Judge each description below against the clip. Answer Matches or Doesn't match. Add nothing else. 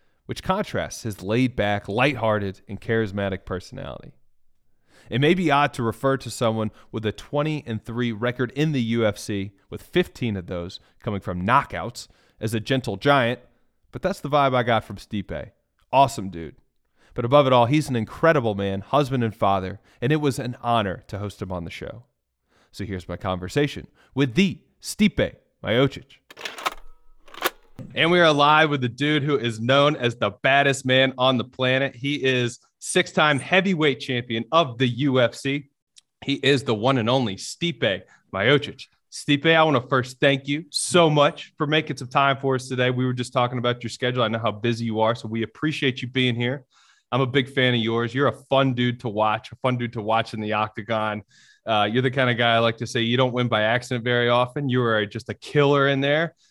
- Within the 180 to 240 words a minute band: Matches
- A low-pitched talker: Matches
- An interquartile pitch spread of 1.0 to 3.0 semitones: Doesn't match